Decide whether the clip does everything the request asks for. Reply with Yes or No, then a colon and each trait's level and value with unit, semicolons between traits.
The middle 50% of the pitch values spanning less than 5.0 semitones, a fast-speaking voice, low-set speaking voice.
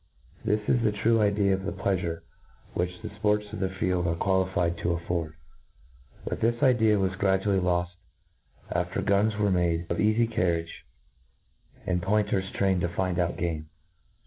No: average, 3.0 semitones; average, 170 wpm; very low, 95 Hz